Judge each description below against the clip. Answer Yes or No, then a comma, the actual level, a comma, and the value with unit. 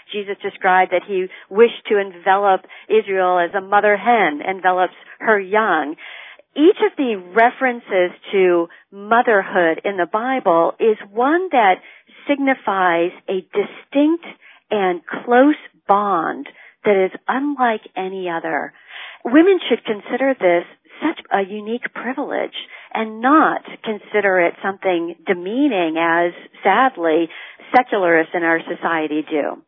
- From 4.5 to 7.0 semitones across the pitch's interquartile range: Yes, wide, 5.5 semitones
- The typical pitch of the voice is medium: No, high, 205 Hz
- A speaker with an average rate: No, slow, 120 wpm